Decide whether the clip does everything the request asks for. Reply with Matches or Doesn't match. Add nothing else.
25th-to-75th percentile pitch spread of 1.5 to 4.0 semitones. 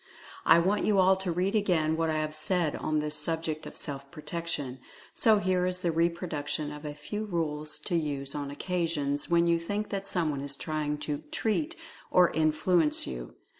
Matches